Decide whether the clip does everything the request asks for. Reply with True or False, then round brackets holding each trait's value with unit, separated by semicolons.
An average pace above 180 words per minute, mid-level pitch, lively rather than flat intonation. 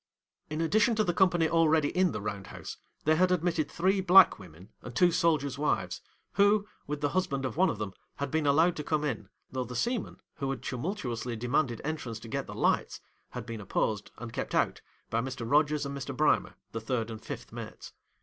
True (205 wpm; 145 Hz; 6.1 semitones)